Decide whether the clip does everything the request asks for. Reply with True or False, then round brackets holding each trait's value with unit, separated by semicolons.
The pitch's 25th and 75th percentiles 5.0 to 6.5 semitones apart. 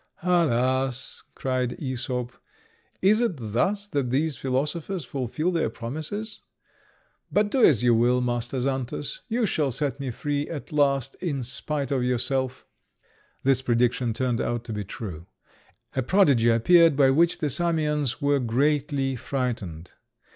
False (3.7 semitones)